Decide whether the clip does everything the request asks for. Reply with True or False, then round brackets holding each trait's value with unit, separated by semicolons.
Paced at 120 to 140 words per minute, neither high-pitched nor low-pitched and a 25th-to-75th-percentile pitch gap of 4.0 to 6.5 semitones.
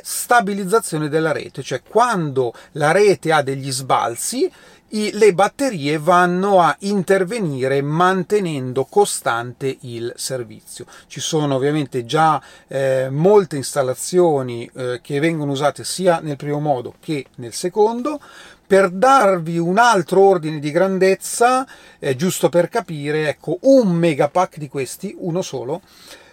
True (125 wpm; 170 Hz; 5.6 semitones)